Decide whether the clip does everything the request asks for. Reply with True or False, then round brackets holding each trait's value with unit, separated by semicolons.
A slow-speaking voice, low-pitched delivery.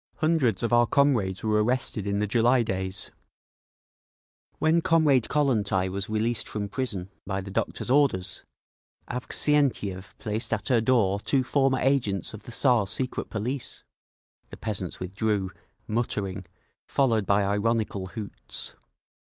True (130 wpm; 110 Hz)